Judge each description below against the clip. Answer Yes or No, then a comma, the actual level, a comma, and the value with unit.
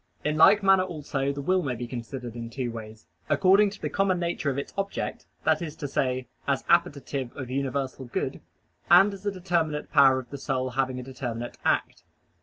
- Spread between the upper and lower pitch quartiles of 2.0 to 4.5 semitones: No, average, 5.3 semitones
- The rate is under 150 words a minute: No, average, 200 wpm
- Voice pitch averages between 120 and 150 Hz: Yes, medium, 140 Hz